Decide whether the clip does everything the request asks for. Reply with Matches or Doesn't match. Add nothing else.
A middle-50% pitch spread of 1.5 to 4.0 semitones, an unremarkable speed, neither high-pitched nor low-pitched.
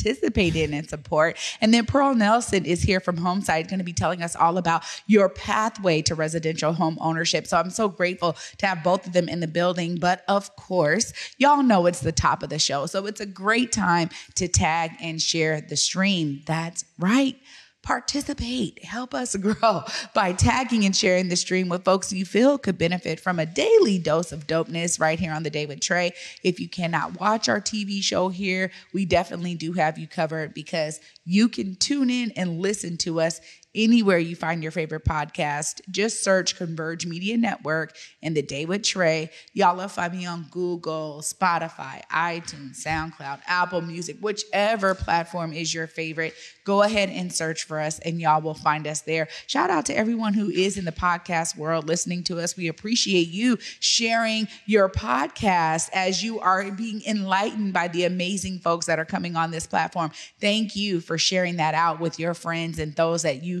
Matches